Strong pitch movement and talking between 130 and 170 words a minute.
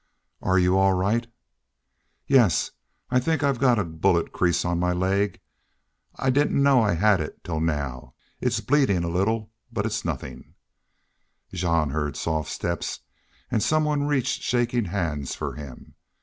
Yes: wide, 6.5 semitones; average, 155 wpm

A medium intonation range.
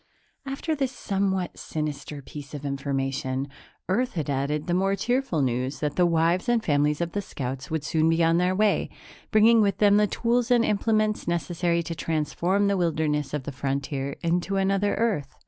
No: wide, 5.7 semitones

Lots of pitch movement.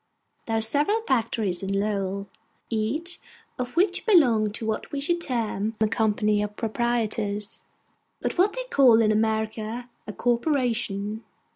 No: average, 3.4 semitones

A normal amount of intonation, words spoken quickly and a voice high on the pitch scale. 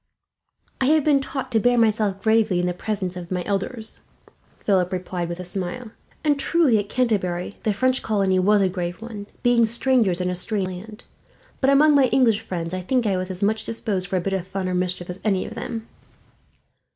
Yes: average, 4.2 semitones; fast, 210 wpm; high, 205 Hz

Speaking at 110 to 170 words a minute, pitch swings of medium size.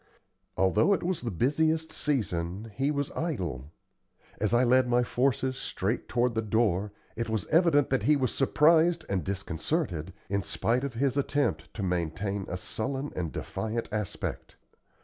No: average, 155 wpm; wide, 6.2 semitones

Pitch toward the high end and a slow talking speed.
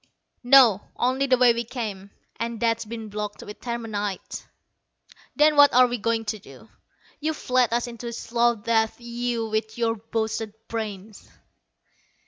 No: high, 230 Hz; average, 150 wpm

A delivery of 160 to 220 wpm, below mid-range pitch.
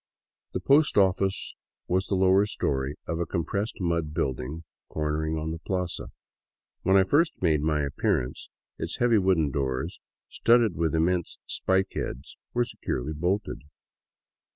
No: average, 150 wpm; very low, 85 Hz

